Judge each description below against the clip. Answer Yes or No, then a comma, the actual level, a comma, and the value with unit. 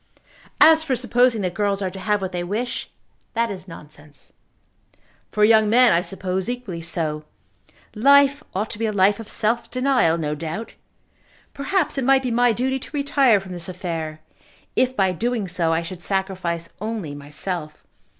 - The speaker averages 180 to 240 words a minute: No, average, 170 wpm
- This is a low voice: No, high, 200 Hz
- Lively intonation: Yes, wide, 6.0 semitones